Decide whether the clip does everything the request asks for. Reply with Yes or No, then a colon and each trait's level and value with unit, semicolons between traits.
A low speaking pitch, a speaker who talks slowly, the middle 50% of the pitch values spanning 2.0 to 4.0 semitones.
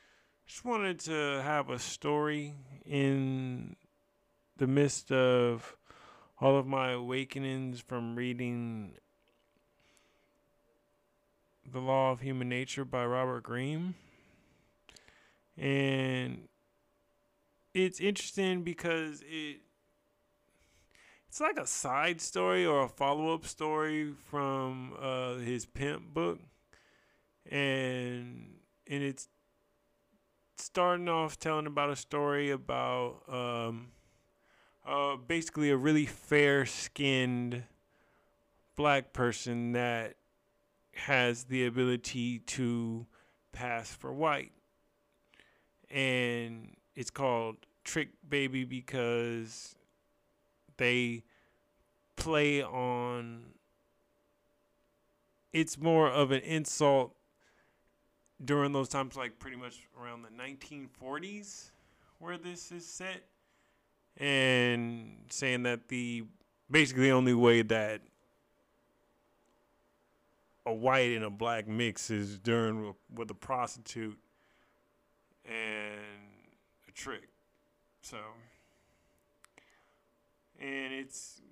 Yes: low, 130 Hz; slow, 90 wpm; average, 3.1 semitones